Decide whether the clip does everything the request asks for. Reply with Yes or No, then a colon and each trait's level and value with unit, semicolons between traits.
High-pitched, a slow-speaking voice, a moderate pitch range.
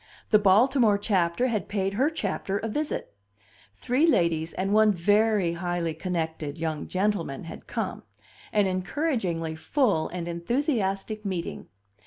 Yes: high, 195 Hz; slow, 130 wpm; average, 4.4 semitones